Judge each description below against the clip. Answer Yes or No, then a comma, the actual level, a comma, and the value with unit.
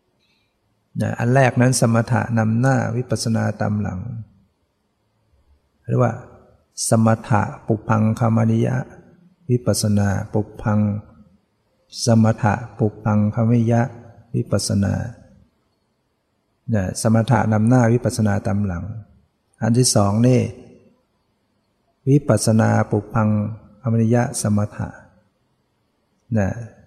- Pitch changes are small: Yes, narrow, 2.1 semitones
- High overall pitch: No, low, 110 Hz